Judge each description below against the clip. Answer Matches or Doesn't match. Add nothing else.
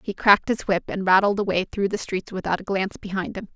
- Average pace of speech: Doesn't match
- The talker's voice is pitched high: Matches